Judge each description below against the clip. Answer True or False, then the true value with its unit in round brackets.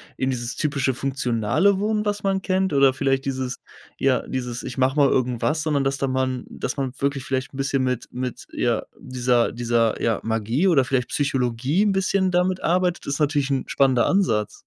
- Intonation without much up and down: False (3.7 semitones)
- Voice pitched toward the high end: False (135 Hz)